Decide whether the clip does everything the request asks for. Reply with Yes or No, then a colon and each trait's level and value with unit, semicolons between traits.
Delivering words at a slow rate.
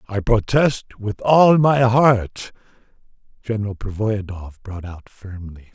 Yes: slow, 115 wpm